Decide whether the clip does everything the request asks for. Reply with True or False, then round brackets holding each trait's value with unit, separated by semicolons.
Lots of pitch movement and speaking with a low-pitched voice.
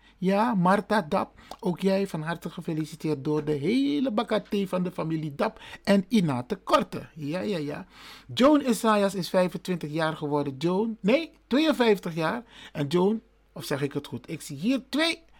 False (5.7 semitones; 190 Hz)